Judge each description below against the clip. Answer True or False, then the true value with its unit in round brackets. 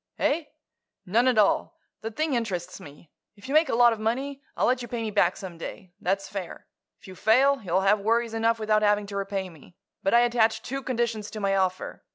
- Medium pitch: False (215 Hz)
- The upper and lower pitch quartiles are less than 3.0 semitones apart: False (3.5 semitones)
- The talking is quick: True (220 wpm)